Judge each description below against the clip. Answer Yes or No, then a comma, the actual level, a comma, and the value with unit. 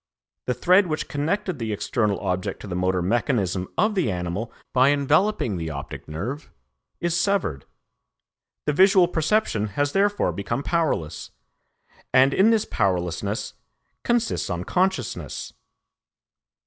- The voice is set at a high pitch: No, low, 135 Hz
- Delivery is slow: Yes, slow, 120 wpm